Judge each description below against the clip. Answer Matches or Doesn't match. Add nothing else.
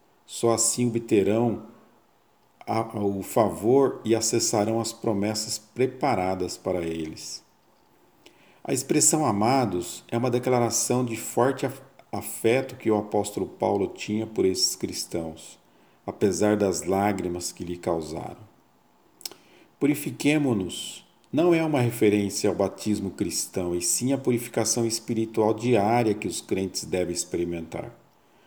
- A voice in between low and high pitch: Doesn't match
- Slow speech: Matches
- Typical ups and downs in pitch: Matches